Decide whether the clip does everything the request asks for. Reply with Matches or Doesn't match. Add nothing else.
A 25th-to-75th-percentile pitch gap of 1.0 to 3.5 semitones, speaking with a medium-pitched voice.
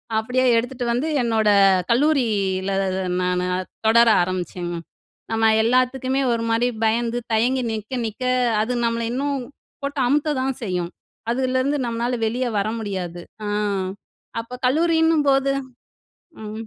Doesn't match